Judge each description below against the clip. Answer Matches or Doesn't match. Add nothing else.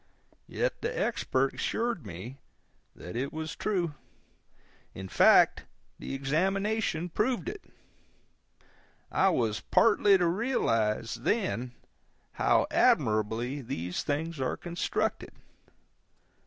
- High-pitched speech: Doesn't match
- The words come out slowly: Matches